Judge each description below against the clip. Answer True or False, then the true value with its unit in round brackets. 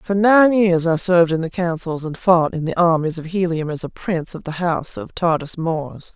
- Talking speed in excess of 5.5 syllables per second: False (5.1 syllables/s)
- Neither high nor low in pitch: True (170 Hz)